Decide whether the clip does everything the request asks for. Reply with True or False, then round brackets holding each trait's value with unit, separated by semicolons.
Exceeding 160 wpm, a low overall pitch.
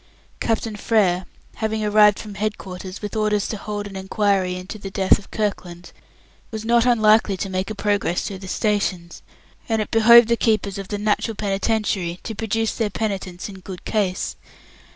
False (175 wpm; 205 Hz)